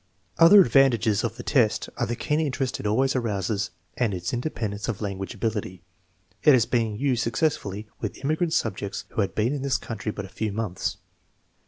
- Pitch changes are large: No, average, 4.3 semitones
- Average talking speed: Yes, average, 185 wpm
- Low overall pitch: Yes, low, 115 Hz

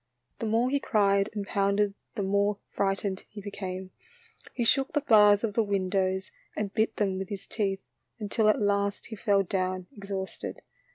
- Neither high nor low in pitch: No, high, 200 Hz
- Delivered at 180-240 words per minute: No, average, 170 wpm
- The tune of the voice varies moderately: No, narrow, 1.6 semitones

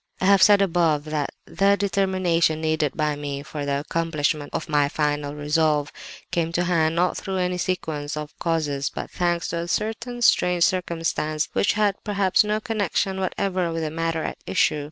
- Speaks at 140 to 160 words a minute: No, average, 175 wpm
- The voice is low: No, medium, 165 Hz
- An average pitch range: Yes, average, 3.6 semitones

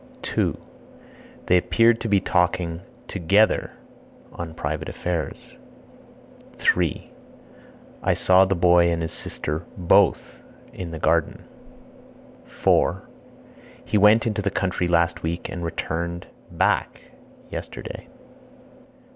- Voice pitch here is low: Yes, very low, 85 Hz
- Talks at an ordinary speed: No, slow, 105 wpm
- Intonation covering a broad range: No, narrow, 2.6 semitones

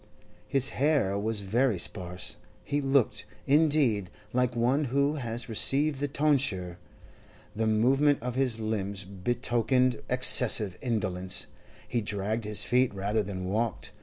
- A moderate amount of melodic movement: Yes, average, 4.8 semitones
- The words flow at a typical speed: No, slow, 130 wpm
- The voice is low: Yes, low, 115 Hz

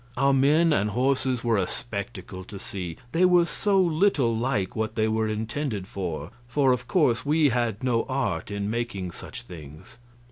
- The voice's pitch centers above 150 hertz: No, low, 120 Hz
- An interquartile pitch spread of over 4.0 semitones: Yes, average, 5.3 semitones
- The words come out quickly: No, average, 175 wpm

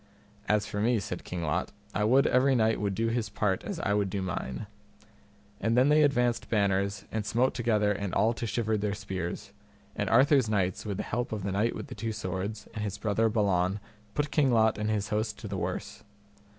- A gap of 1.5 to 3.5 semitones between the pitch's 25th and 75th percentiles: Yes, narrow, 2.6 semitones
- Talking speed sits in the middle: No, fast, 215 wpm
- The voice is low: Yes, low, 105 Hz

